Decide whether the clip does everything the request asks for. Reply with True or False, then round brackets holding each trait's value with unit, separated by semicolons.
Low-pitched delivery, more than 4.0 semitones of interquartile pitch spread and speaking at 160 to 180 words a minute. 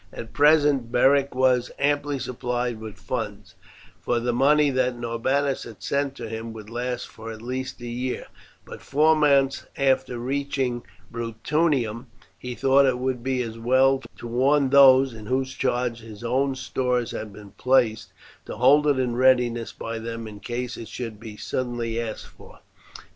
False (125 Hz; 2.6 semitones; 165 wpm)